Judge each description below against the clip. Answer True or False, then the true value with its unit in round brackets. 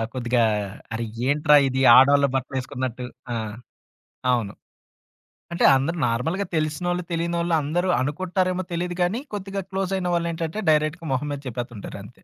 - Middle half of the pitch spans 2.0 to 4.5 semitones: False (5.2 semitones)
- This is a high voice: False (155 Hz)